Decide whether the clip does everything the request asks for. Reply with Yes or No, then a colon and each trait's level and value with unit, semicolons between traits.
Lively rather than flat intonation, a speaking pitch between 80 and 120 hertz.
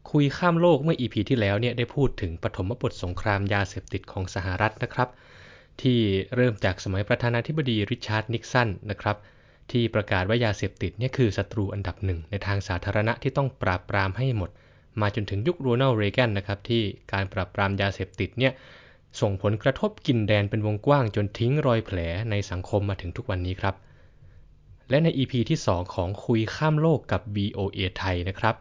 No: average, 4.0 semitones; low, 105 Hz